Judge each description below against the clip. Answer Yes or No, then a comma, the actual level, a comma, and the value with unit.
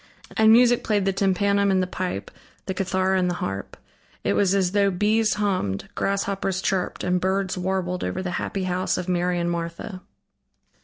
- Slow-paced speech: No, average, 175 wpm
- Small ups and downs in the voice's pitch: Yes, narrow, 1.7 semitones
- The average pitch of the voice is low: No, high, 190 Hz